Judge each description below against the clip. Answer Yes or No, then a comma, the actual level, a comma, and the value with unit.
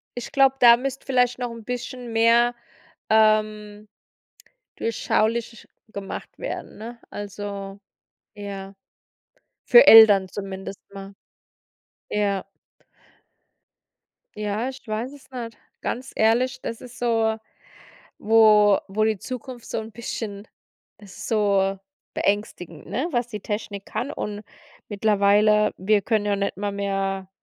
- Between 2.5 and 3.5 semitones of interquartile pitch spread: Yes, average, 2.8 semitones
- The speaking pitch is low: No, high, 215 Hz